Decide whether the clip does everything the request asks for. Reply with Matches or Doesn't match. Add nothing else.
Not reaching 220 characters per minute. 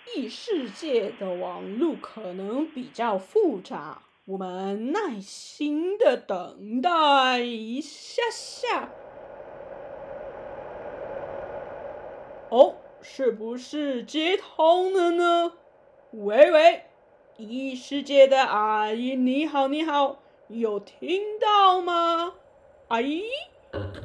Matches